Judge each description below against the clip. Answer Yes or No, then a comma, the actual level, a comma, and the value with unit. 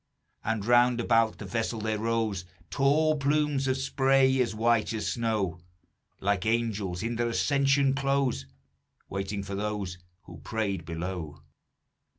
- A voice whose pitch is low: Yes, low, 115 Hz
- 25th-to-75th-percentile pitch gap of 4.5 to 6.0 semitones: Yes, average, 5.0 semitones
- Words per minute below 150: Yes, slow, 135 wpm